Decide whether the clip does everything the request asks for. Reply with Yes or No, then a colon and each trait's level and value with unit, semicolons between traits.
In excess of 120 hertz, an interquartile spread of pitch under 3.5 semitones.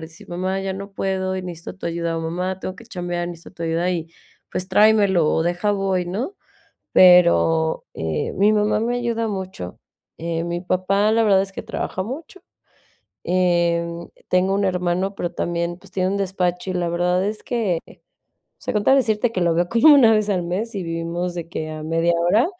Yes: medium, 185 Hz; average, 2.7 semitones